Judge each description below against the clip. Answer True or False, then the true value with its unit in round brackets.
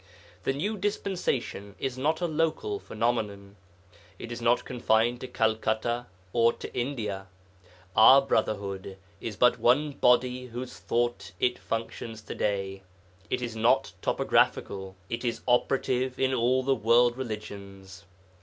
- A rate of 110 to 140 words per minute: True (135 wpm)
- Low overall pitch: True (120 Hz)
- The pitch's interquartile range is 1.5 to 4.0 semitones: True (3.2 semitones)